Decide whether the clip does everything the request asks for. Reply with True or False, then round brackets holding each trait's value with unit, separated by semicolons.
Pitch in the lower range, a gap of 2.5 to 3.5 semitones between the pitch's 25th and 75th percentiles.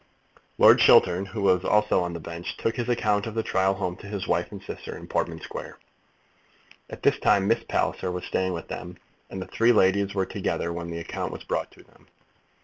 True (95 Hz; 2.8 semitones)